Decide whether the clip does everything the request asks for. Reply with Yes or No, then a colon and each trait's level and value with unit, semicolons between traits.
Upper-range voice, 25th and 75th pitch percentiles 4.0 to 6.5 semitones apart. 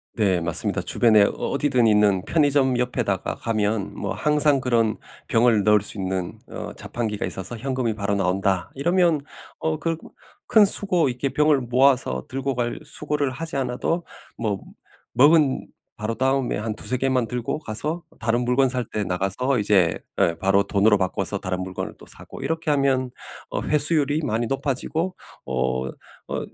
No: low, 125 Hz; average, 5.2 semitones